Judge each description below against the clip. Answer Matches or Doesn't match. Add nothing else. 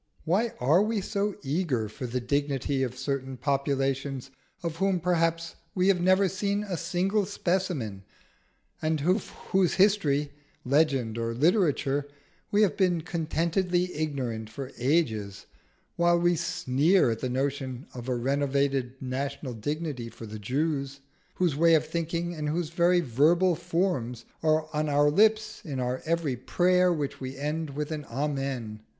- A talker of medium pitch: Matches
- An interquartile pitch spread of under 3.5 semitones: Doesn't match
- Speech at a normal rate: Matches